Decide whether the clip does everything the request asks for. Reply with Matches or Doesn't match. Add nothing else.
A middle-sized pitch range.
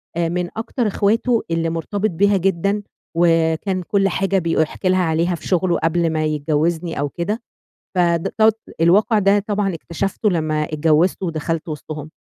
Matches